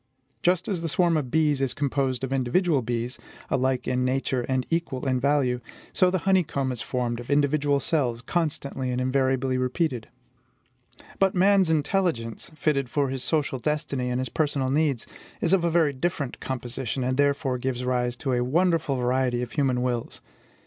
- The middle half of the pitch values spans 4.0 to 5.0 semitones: No, average, 3.4 semitones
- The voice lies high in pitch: No, low, 135 Hz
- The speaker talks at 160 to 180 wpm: Yes, average, 170 wpm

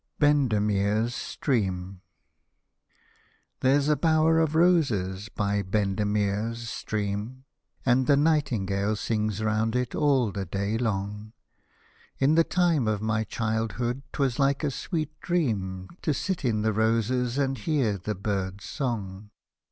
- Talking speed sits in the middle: No, slow, 125 wpm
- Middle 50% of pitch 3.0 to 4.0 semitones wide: No, average, 5.1 semitones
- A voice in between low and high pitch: No, low, 110 Hz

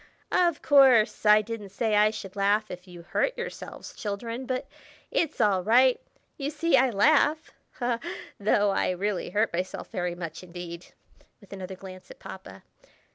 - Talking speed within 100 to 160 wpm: Yes, average, 155 wpm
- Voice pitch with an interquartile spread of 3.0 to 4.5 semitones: No, average, 5.2 semitones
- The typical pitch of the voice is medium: No, high, 210 Hz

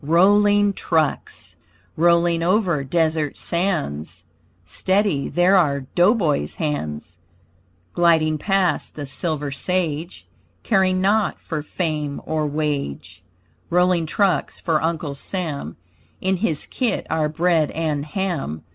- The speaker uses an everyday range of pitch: Yes, average, 4.0 semitones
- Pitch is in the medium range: Yes, medium, 160 Hz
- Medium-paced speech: No, slow, 110 wpm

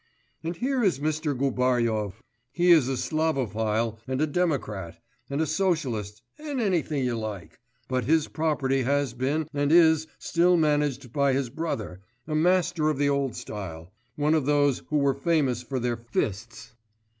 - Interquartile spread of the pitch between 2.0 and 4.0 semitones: No, average, 4.8 semitones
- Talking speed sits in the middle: Yes, average, 160 wpm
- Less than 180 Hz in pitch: Yes, medium, 140 Hz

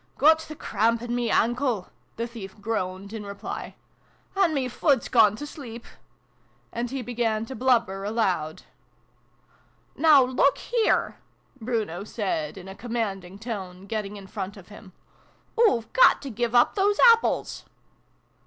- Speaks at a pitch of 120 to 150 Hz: No, high, 225 Hz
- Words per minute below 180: Yes, average, 170 wpm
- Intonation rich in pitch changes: No, average, 4.3 semitones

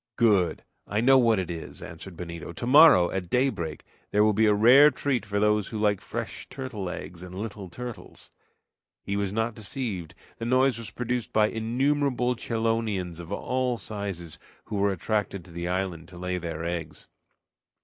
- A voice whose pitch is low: Yes, low, 105 Hz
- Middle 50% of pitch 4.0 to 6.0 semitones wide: Yes, average, 4.8 semitones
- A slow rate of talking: No, average, 170 wpm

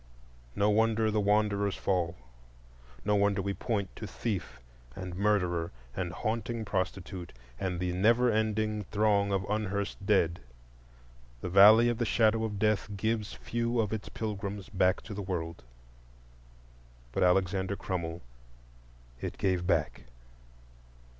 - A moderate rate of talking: No, slow, 130 wpm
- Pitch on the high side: No, low, 100 Hz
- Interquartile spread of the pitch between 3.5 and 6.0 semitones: No, average, 2.7 semitones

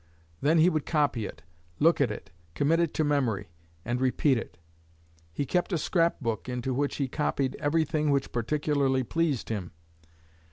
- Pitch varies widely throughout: No, average, 3.9 semitones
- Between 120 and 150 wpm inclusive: No, average, 165 wpm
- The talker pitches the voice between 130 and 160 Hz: Yes, medium, 140 Hz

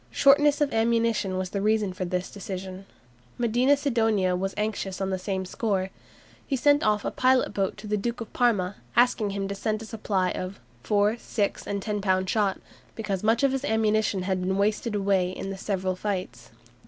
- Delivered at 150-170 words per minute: No, average, 190 wpm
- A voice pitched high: Yes, high, 205 Hz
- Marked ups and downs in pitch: No, average, 3.0 semitones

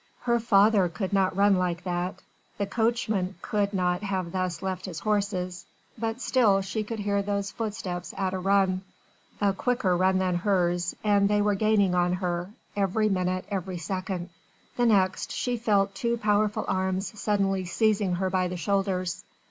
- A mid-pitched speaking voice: No, high, 195 Hz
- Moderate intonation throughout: No, narrow, 2.2 semitones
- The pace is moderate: Yes, average, 165 wpm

